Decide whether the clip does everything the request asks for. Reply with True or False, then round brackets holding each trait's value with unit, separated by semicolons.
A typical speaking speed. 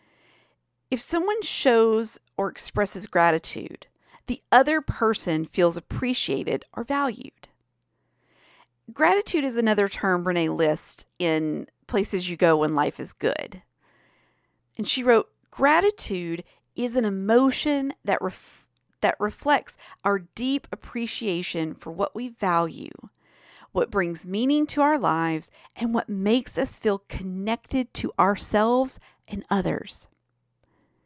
False (120 wpm)